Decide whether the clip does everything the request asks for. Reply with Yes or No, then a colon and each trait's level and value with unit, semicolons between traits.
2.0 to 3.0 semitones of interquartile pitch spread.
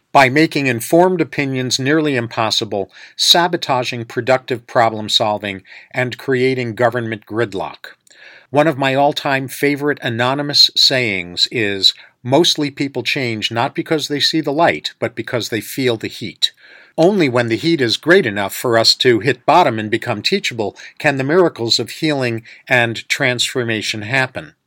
No: average, 4.0 semitones